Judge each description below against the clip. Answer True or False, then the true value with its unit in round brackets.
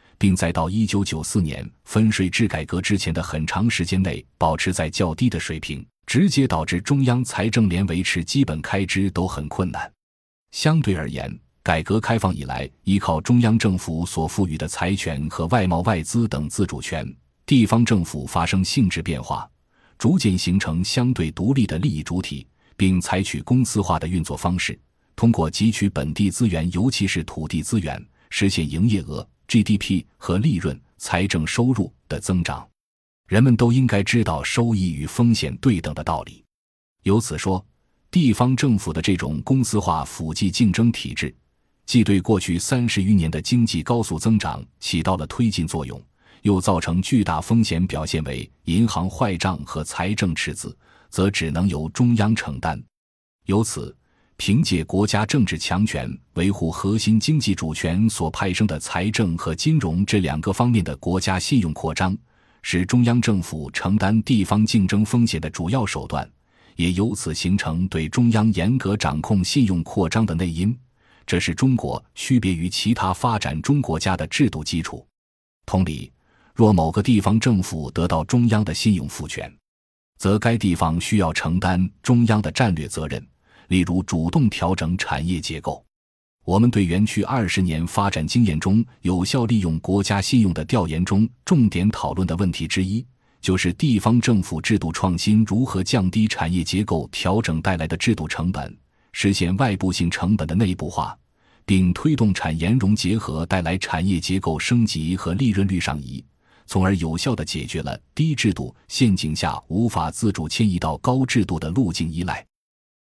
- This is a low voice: True (95 Hz)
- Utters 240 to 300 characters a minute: True (260 characters per minute)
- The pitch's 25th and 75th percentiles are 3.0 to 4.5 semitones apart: False (5.2 semitones)